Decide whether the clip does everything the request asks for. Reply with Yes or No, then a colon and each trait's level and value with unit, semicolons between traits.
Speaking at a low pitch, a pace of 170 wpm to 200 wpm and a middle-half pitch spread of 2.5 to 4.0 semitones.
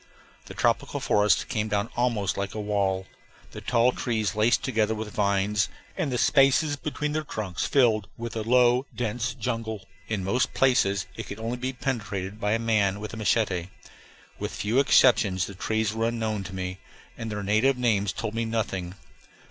Yes: low, 110 Hz; average, 180 wpm; average, 3.2 semitones